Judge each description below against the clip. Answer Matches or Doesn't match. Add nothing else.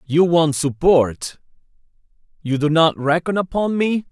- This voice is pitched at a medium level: Matches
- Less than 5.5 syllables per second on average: Matches